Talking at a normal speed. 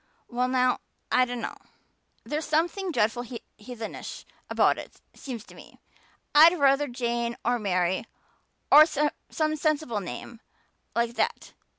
No: slow, 120 wpm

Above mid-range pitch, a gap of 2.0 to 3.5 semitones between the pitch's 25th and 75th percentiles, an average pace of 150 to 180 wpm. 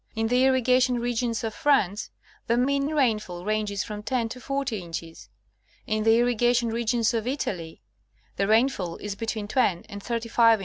Yes: high, 230 Hz; average, 2.9 semitones; average, 170 wpm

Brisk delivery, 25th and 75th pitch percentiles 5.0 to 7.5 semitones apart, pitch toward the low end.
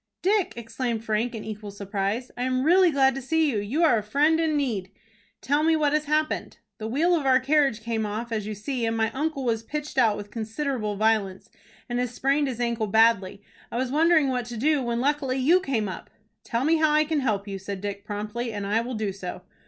No: fast, 230 wpm; average, 5.3 semitones; high, 240 Hz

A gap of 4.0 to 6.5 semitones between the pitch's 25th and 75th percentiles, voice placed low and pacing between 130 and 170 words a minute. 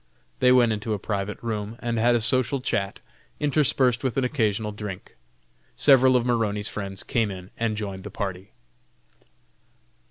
No: average, 3.3 semitones; low, 110 Hz; average, 155 wpm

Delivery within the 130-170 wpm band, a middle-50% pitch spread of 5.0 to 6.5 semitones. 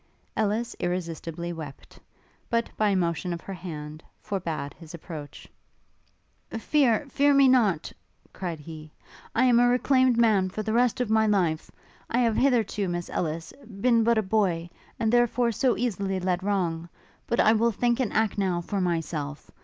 Yes: average, 165 wpm; wide, 5.5 semitones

